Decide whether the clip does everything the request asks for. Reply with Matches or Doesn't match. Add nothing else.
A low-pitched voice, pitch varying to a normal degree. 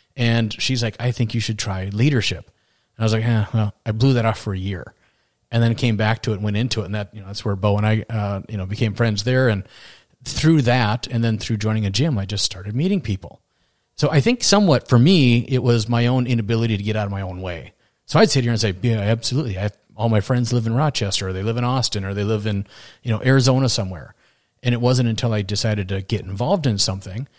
Matches